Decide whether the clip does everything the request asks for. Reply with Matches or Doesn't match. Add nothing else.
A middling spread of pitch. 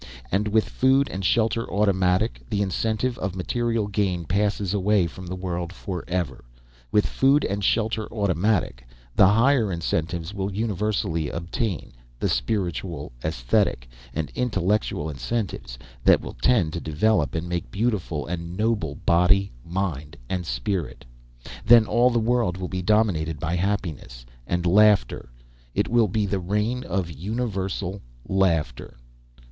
Matches